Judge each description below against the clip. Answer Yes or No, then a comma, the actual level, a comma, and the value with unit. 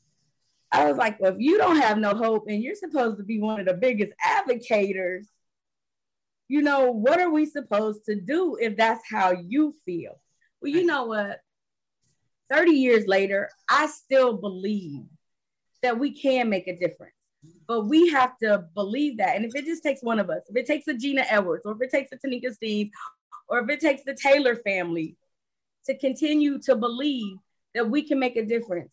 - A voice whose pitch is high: Yes, high, 235 Hz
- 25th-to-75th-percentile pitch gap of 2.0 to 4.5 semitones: No, wide, 5.6 semitones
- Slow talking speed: No, average, 195 wpm